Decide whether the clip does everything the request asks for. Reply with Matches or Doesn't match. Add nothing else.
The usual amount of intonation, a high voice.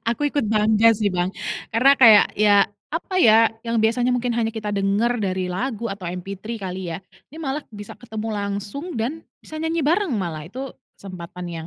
Matches